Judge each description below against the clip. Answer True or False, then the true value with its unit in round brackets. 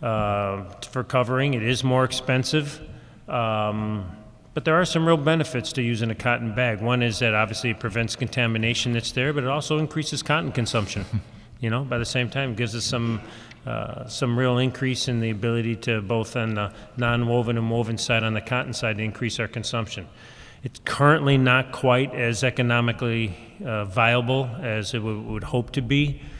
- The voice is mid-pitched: False (120 Hz)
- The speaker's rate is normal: True (190 wpm)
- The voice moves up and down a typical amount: False (2.3 semitones)